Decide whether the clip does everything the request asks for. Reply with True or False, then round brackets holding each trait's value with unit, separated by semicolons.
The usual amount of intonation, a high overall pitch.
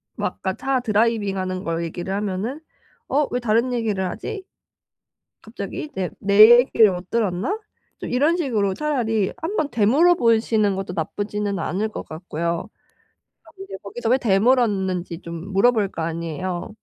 True (4.8 semitones; 210 Hz)